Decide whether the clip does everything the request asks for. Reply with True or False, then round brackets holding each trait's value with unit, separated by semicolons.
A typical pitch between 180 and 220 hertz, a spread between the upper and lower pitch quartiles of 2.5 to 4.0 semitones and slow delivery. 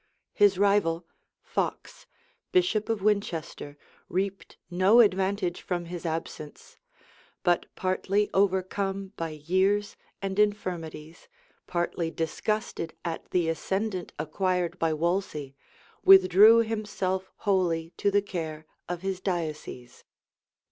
True (185 Hz; 3.3 semitones; 105 wpm)